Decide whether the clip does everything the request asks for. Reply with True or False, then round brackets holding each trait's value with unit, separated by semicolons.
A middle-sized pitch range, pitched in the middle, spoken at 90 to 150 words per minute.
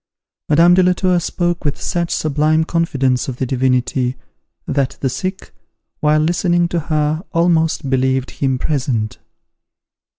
True (4.4 semitones; 150 Hz; 135 wpm)